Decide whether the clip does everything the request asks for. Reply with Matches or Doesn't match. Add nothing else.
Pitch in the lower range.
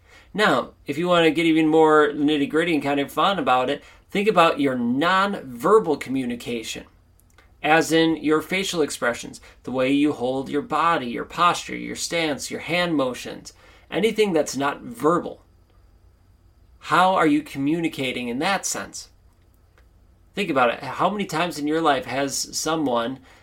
Doesn't match